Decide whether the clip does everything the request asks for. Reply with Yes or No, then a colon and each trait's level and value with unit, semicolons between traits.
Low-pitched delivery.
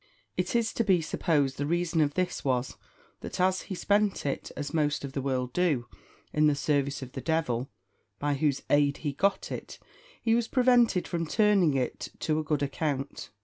No: medium, 155 Hz